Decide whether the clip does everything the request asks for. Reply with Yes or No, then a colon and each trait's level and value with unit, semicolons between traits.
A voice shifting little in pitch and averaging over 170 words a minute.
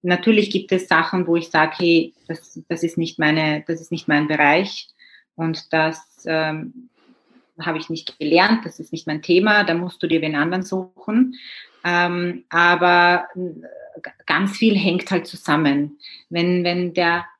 No: narrow, 2.2 semitones; average, 160 wpm